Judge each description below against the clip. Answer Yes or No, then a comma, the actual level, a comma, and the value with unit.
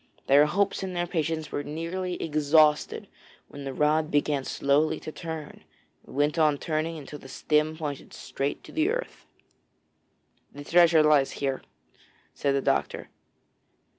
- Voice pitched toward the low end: No, medium, 155 Hz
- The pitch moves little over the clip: Yes, narrow, 2.2 semitones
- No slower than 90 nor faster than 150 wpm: Yes, average, 145 wpm